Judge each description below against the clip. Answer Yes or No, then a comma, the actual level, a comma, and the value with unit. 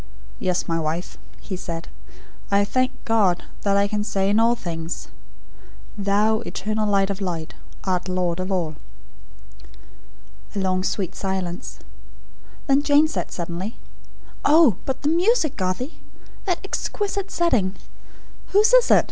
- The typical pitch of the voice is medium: No, high, 200 Hz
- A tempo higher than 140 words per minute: No, slow, 135 wpm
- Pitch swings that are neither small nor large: No, wide, 5.8 semitones